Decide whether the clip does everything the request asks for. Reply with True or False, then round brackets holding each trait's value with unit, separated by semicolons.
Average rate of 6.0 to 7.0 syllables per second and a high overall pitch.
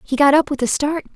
True (6.5 syllables/s; 285 Hz)